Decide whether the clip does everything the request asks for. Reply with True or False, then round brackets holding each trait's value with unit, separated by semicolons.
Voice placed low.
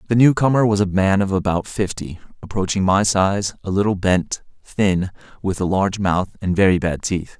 True (95 Hz)